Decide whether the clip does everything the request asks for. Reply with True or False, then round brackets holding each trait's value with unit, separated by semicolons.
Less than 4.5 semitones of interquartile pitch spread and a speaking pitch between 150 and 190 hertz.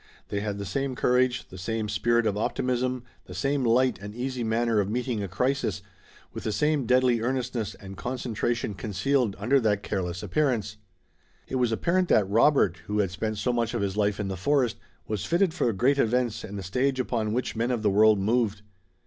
False (3.6 semitones; 115 Hz)